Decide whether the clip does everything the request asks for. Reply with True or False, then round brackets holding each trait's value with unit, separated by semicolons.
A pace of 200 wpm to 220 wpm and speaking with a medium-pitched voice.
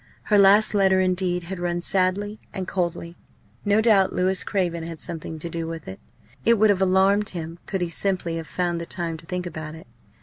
True (205 wpm; 180 Hz)